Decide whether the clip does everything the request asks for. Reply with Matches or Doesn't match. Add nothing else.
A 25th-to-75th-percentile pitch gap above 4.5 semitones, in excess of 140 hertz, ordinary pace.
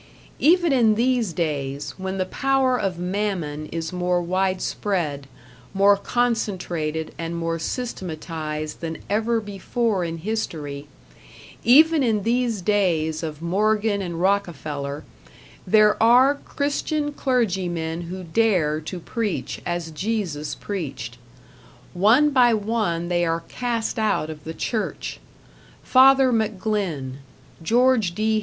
Doesn't match